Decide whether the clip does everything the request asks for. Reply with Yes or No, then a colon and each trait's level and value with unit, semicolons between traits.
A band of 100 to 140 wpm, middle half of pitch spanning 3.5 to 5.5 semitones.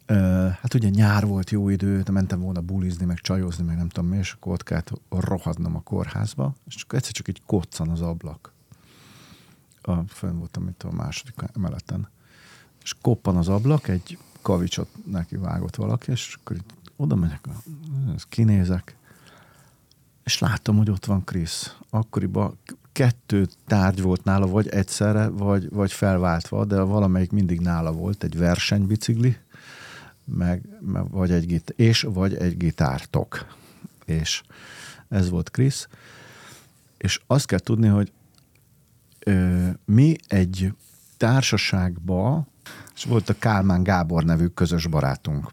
Yes: average, 135 wpm; average, 3.8 semitones